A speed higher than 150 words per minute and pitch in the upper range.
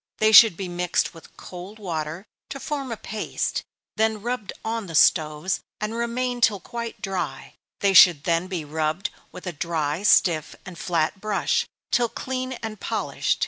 Yes: average, 165 wpm; high, 195 Hz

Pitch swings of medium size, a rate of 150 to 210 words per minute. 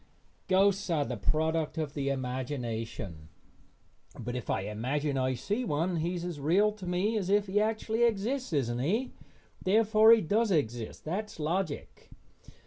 No: wide, 7.8 semitones; average, 155 wpm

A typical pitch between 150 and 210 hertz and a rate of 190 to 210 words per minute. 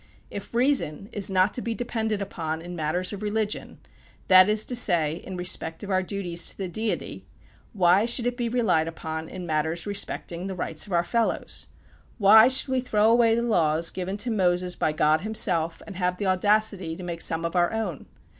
Yes: high, 190 Hz; average, 200 wpm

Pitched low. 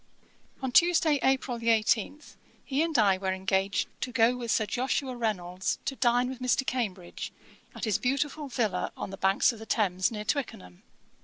No: high, 235 Hz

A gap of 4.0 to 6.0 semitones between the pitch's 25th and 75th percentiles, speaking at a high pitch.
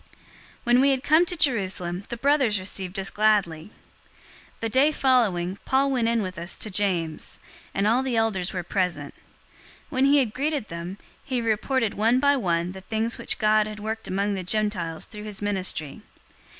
Yes: average, 5.2 semitones; high, 215 Hz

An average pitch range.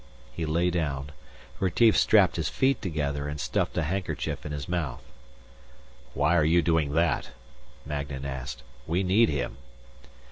Yes: average, 3.7 semitones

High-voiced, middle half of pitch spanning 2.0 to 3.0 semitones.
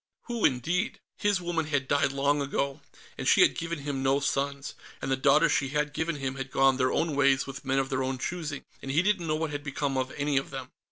No: medium, 140 Hz; narrow, 2.4 semitones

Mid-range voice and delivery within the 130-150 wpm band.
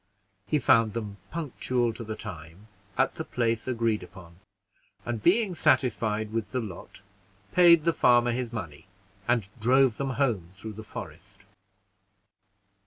No: low, 115 Hz; average, 140 wpm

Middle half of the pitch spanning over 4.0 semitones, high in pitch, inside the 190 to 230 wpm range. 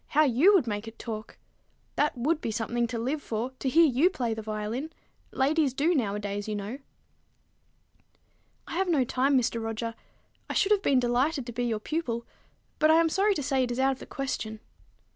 Yes: average, 5.1 semitones; very high, 255 Hz; average, 200 wpm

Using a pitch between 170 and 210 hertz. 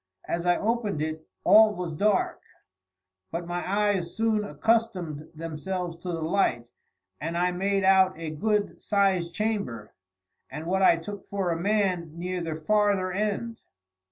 Yes: medium, 185 Hz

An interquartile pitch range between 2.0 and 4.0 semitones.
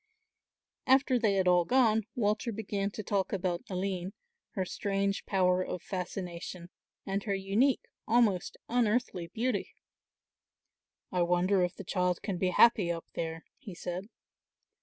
Yes: average, 3.0 semitones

